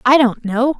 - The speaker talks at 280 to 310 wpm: No, fast, 225 wpm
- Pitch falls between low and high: No, very high, 250 Hz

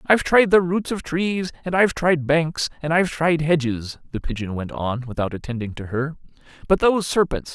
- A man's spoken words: Yes, male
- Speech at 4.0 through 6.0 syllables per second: Yes, 5.3 syllables/s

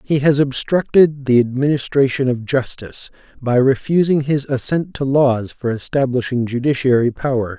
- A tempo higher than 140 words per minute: No, slow, 135 wpm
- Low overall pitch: Yes, low, 130 Hz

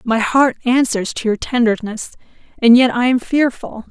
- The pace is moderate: Yes, average, 170 wpm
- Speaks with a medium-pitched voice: No, high, 240 Hz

